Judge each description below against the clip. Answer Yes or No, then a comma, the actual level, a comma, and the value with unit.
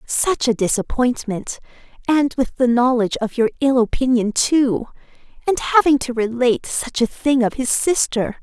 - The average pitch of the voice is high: Yes, very high, 250 Hz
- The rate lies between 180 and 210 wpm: No, average, 155 wpm